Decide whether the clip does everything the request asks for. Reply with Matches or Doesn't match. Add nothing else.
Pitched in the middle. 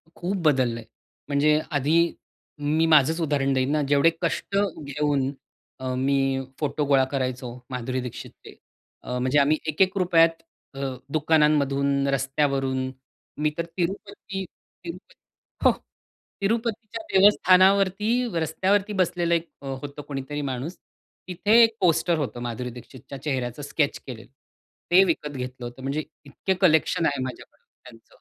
Matches